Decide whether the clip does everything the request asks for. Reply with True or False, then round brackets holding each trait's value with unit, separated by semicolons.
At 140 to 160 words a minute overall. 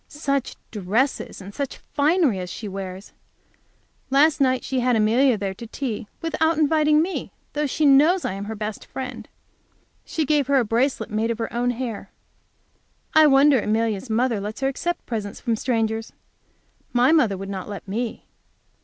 False (170 wpm)